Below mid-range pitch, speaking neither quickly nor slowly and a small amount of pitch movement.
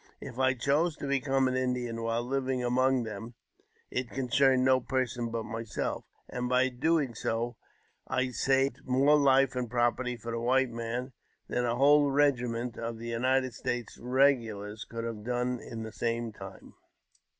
Yes: low, 125 Hz; average, 160 wpm; narrow, 2.2 semitones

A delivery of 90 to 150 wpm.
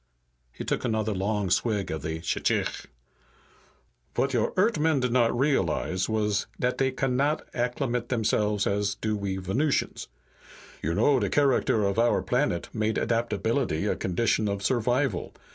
Yes: average, 140 wpm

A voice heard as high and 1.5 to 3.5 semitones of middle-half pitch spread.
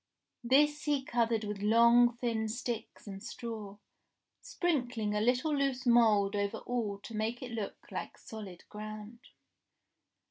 Yes: high, 230 Hz; narrow, 2.6 semitones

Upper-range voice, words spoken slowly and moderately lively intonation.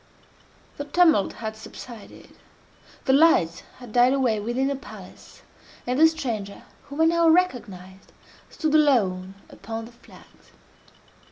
No: high, 245 Hz; slow, 125 wpm; wide, 6.0 semitones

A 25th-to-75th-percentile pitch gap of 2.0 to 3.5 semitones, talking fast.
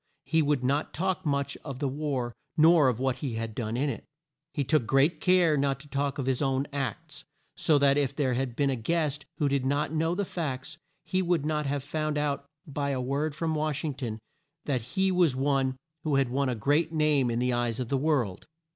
Yes: average, 2.7 semitones; fast, 225 wpm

